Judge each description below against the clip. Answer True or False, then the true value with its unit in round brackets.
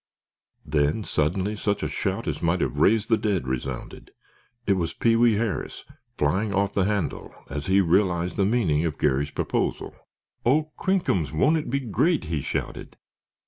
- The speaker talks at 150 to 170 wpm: True (165 wpm)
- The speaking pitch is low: True (95 Hz)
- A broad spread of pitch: True (5.7 semitones)